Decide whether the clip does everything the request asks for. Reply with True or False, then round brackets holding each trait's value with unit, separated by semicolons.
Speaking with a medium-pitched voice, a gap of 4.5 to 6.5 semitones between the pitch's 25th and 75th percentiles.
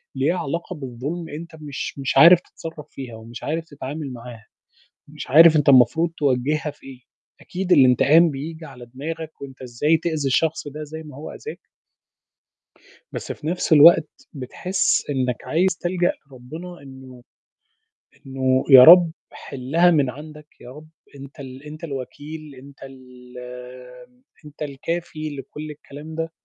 False (150 Hz; 3.3 semitones)